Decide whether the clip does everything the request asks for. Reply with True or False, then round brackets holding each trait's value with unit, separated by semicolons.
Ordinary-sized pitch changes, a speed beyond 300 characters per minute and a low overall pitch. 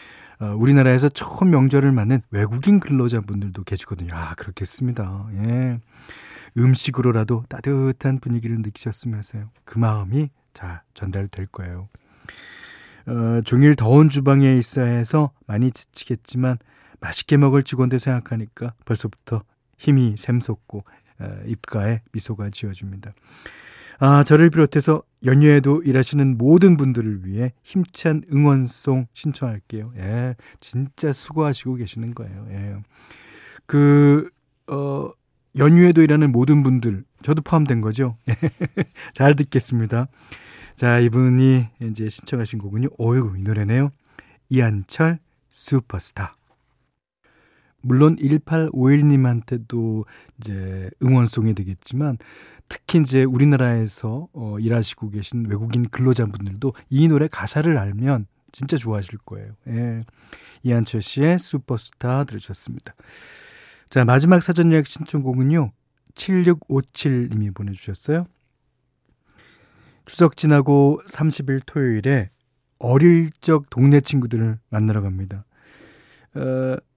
False (4.2 semitones; 265 characters per minute; 125 Hz)